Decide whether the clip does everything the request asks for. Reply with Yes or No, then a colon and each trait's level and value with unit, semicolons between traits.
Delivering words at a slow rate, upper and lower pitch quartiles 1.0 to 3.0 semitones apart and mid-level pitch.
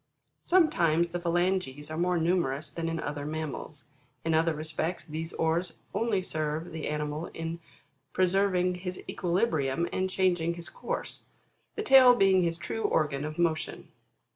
No: average, 150 wpm; average, 2.7 semitones; medium, 170 Hz